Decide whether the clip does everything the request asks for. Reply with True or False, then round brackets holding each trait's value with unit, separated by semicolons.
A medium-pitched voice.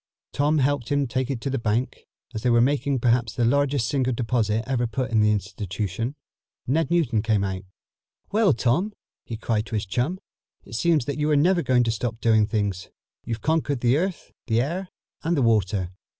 False (120 Hz)